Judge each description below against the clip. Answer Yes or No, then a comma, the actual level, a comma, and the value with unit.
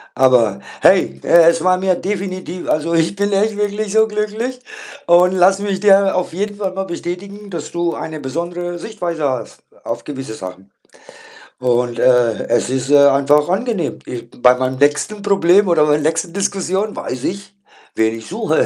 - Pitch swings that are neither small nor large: No, wide, 6.1 semitones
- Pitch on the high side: No, medium, 175 Hz